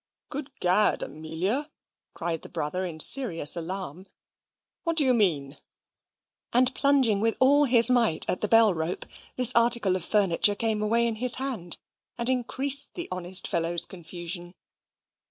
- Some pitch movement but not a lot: No, wide, 6.3 semitones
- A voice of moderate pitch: No, high, 210 Hz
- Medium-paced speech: Yes, average, 150 wpm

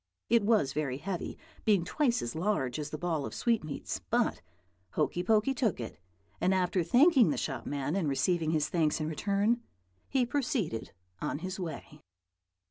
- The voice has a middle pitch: Yes, medium, 180 Hz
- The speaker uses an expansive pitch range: Yes, wide, 6.3 semitones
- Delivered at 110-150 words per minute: No, average, 165 wpm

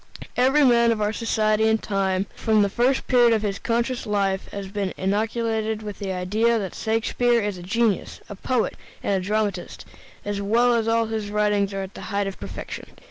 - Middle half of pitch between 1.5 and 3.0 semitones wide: Yes, narrow, 2.4 semitones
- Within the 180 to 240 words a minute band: Yes, average, 190 wpm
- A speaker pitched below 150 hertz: No, high, 215 Hz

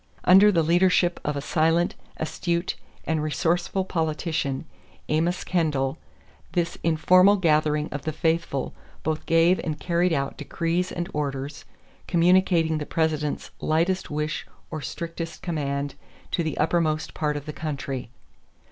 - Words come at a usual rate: No, slow, 130 wpm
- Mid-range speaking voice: Yes, medium, 160 Hz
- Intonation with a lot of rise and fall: No, narrow, 2.4 semitones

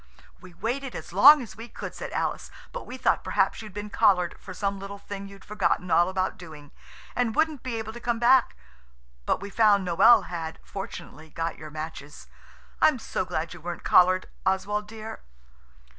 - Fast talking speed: No, average, 185 wpm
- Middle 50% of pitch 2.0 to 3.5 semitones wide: No, average, 4.2 semitones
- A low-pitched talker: No, high, 200 Hz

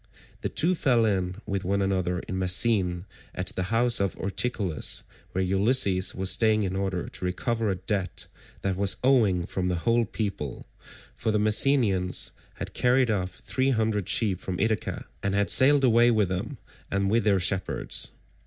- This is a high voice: No, low, 100 Hz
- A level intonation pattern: No, average, 3.7 semitones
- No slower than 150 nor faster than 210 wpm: Yes, average, 170 wpm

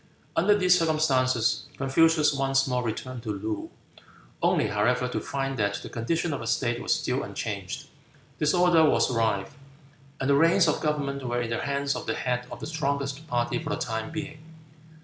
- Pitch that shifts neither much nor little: Yes, average, 4.1 semitones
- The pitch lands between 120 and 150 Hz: Yes, low, 135 Hz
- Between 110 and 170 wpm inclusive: No, average, 180 wpm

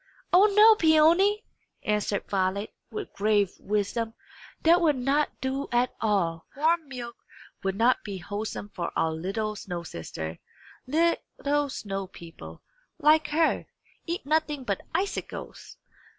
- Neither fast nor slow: No, slow, 125 wpm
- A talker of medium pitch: No, high, 240 Hz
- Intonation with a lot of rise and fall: Yes, wide, 7.8 semitones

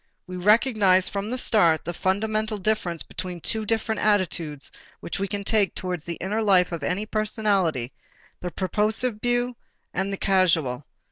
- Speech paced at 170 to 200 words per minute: No, average, 155 wpm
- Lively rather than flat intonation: No, average, 3.3 semitones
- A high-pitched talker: Yes, high, 195 Hz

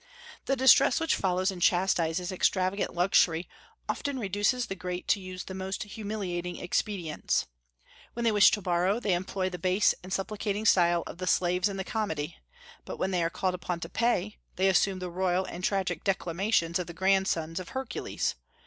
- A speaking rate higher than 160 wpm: Yes, average, 180 wpm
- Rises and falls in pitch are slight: Yes, narrow, 2.3 semitones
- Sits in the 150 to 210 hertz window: Yes, medium, 185 Hz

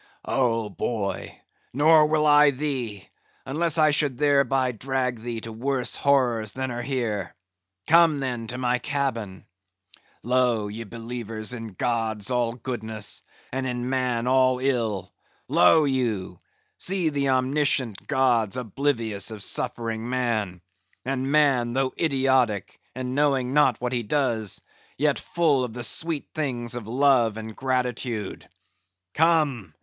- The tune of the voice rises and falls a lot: No, average, 3.3 semitones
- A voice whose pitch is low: Yes, low, 125 Hz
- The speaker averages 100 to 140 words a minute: Yes, slow, 135 wpm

